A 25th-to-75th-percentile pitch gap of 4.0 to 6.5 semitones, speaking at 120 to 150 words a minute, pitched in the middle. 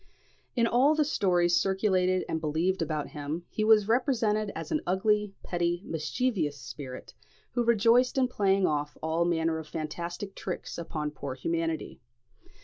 Yes: average, 5.0 semitones; average, 145 wpm; medium, 180 Hz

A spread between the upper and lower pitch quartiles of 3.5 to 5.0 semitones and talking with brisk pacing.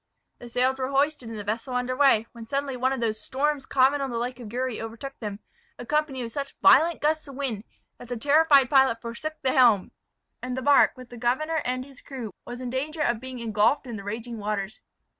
No: average, 3.1 semitones; fast, 220 wpm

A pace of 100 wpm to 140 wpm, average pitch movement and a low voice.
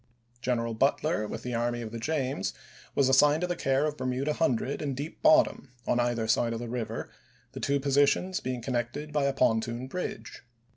No: average, 190 wpm; average, 3.3 semitones; low, 130 Hz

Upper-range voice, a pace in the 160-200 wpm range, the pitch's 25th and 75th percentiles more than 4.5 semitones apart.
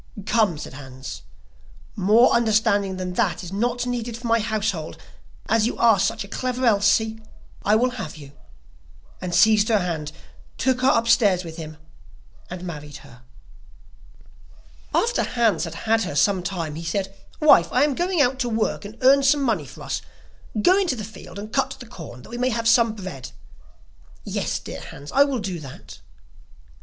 Yes: high, 215 Hz; average, 175 wpm; average, 5.1 semitones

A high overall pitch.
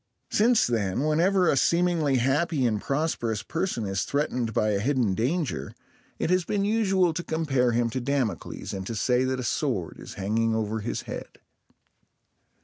No: low, 130 Hz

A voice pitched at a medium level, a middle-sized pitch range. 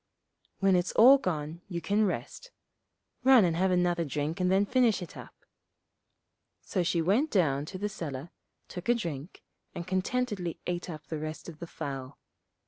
Yes: medium, 180 Hz; average, 4.1 semitones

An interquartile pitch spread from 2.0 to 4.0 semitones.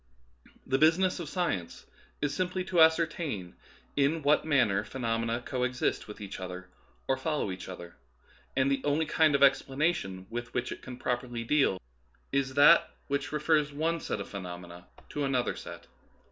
No: average, 5.1 semitones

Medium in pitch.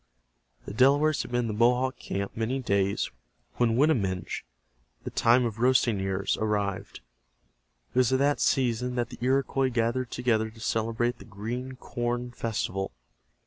No: low, 120 Hz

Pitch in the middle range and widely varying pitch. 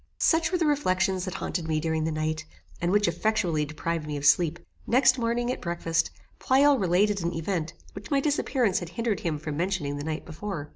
Yes: medium, 180 Hz; wide, 6.3 semitones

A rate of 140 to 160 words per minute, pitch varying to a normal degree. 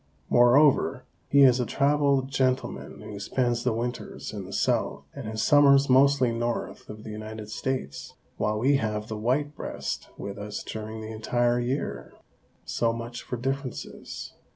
Yes: average, 155 wpm; average, 3.6 semitones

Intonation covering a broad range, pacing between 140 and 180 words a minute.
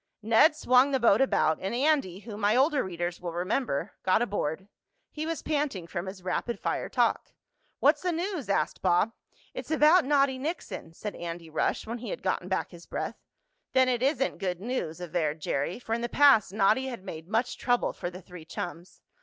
No: wide, 7.0 semitones; average, 195 wpm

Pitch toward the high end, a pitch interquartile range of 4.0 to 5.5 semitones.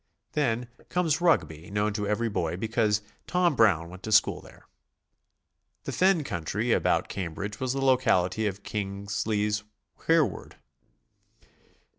No: low, 105 Hz; average, 4.7 semitones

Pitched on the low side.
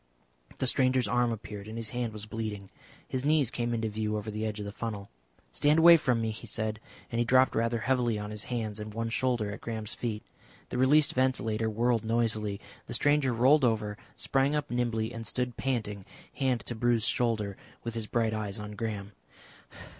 Yes: low, 115 Hz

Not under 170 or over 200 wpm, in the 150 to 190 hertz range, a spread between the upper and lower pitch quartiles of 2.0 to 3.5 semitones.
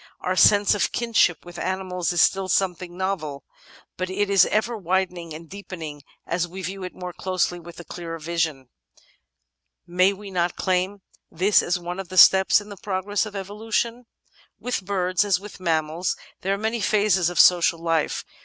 Yes: average, 175 wpm; medium, 185 Hz; narrow, 2.4 semitones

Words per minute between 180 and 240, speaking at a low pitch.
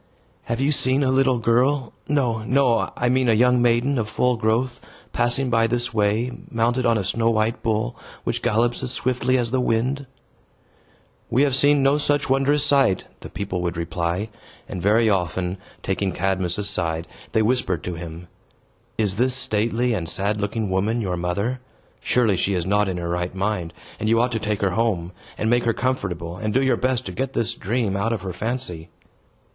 Yes: average, 190 wpm; low, 115 Hz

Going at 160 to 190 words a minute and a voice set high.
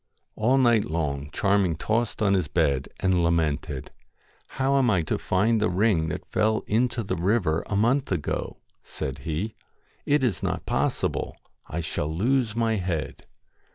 No: average, 170 wpm; low, 100 Hz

